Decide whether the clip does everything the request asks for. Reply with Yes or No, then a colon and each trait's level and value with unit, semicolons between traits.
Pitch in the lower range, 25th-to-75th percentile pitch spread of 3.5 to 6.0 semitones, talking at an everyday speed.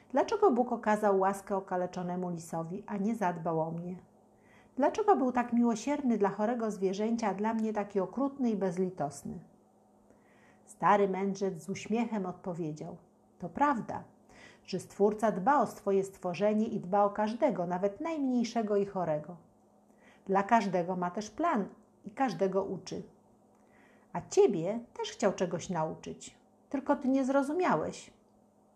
No: high, 205 Hz; average, 3.9 semitones; average, 135 wpm